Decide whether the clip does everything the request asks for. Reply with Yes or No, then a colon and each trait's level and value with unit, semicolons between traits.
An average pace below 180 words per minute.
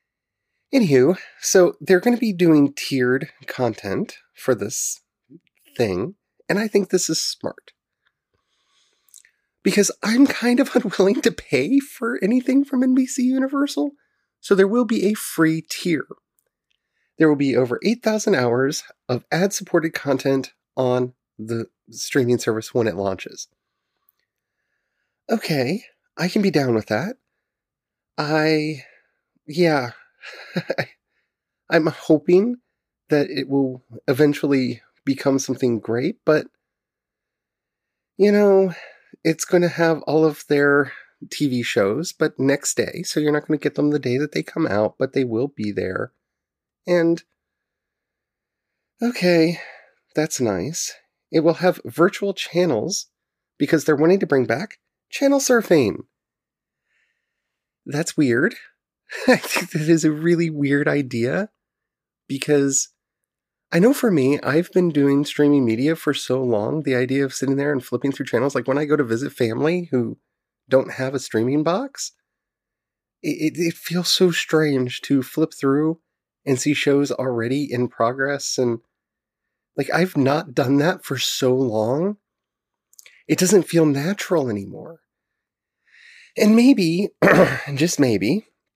Yes: slow, 135 wpm